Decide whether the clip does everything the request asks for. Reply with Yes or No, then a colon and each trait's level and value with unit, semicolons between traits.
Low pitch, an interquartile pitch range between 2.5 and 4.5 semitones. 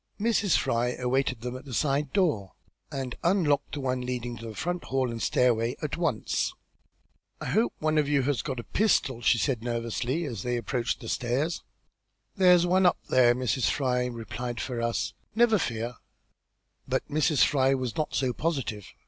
Yes: low, 130 Hz; average, 4.1 semitones